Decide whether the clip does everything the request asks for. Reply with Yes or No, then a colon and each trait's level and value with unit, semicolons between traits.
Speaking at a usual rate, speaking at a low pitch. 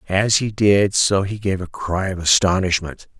Yes: average, 190 wpm; very low, 95 Hz